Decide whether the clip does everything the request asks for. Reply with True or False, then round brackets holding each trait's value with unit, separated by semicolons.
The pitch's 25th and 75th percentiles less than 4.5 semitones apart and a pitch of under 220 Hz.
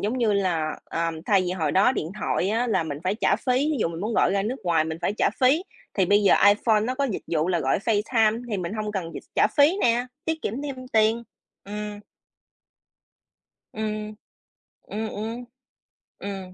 True (4.1 semitones; 210 Hz)